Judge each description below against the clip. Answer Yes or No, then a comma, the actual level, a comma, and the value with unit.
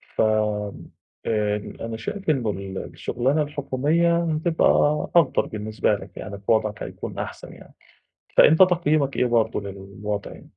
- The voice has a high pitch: No, low, 115 Hz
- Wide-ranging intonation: Yes, wide, 6.6 semitones